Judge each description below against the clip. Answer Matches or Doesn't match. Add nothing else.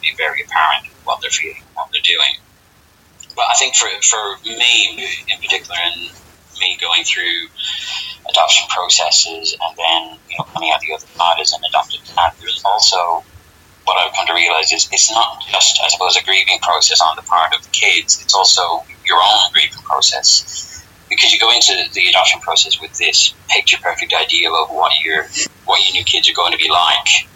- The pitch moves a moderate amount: Doesn't match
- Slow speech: Doesn't match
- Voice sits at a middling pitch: Doesn't match